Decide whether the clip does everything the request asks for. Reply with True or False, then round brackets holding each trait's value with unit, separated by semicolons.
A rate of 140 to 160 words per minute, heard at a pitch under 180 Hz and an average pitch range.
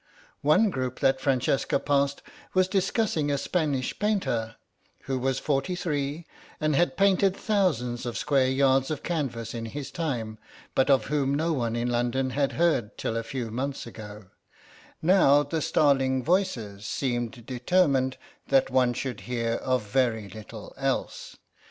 True (150 wpm; 135 Hz; 4.1 semitones)